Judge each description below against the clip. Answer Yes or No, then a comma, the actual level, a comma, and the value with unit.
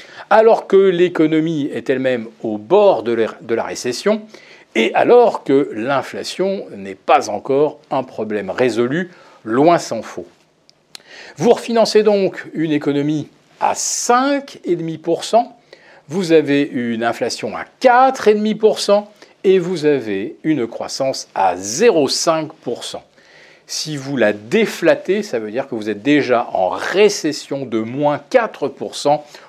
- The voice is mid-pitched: Yes, medium, 155 Hz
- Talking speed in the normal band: No, slow, 120 wpm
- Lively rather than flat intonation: Yes, wide, 7.9 semitones